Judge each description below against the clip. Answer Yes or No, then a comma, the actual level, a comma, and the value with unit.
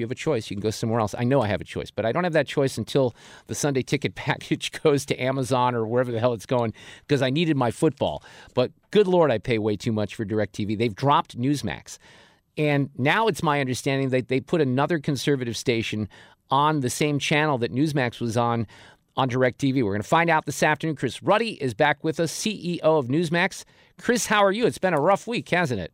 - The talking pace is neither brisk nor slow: No, fast, 235 wpm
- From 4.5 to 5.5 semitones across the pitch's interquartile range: Yes, average, 4.8 semitones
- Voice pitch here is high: No, low, 135 Hz